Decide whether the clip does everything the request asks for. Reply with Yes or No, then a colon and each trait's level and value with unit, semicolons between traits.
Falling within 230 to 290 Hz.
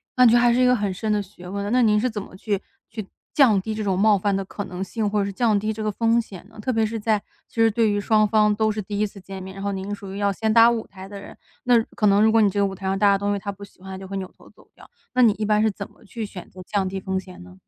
No: high, 205 Hz